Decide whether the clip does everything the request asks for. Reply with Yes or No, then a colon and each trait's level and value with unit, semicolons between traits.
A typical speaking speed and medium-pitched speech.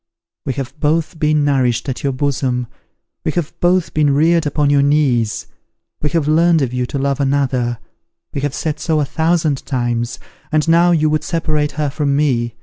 Yes: average, 185 wpm; medium, 145 Hz